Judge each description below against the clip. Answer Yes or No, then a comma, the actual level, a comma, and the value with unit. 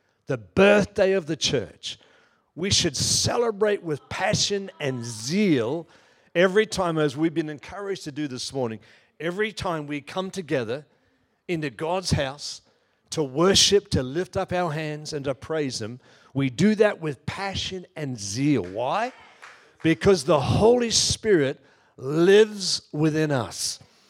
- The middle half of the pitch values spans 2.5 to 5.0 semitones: No, wide, 5.5 semitones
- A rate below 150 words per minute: Yes, average, 140 wpm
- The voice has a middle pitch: Yes, medium, 160 Hz